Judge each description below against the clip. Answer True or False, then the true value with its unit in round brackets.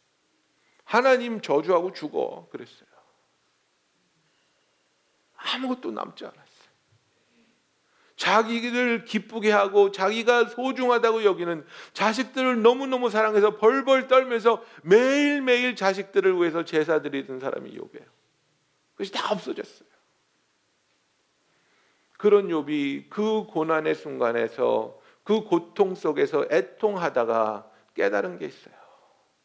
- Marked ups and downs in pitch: True (6.2 semitones)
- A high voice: True (215 Hz)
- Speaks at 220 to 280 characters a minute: True (245 characters per minute)